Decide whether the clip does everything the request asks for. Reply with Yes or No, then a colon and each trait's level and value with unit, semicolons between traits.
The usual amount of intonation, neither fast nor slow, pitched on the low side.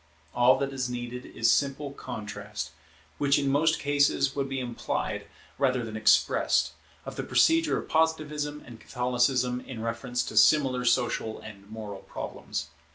Yes: average, 3.4 semitones; average, 150 wpm; low, 125 Hz